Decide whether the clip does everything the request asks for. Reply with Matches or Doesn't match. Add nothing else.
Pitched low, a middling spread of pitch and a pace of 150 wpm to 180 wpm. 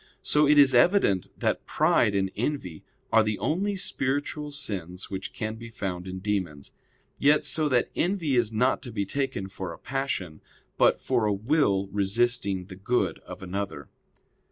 Doesn't match